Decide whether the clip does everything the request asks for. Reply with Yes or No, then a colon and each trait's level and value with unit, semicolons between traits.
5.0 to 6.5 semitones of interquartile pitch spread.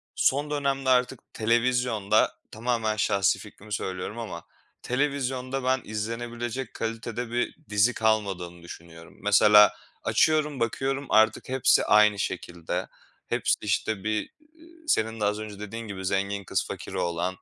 No: average, 3.6 semitones